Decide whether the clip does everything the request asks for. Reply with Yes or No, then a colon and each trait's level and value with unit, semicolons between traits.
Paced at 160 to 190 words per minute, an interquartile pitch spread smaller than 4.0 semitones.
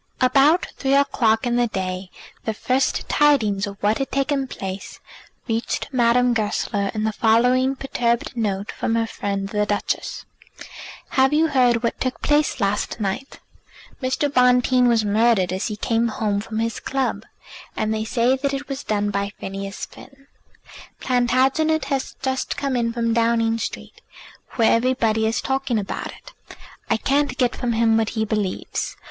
Yes: average, 165 wpm; average, 3.4 semitones